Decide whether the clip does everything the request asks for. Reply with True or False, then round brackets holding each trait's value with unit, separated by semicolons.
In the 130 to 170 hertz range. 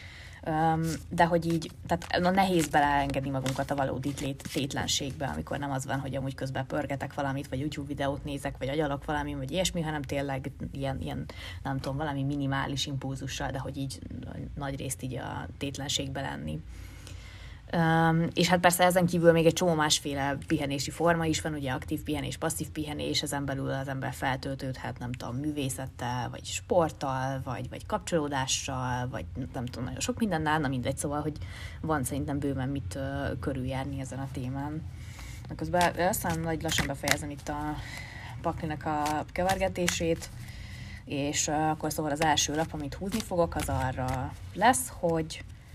True (140 Hz)